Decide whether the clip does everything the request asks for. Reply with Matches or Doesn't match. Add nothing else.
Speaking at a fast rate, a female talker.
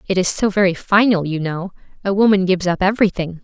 Matches